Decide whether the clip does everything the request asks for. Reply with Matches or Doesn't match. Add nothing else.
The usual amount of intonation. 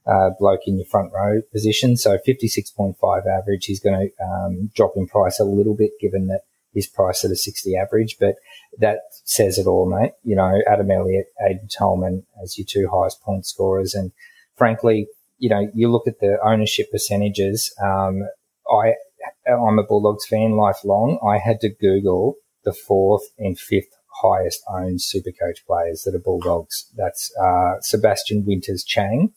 Doesn't match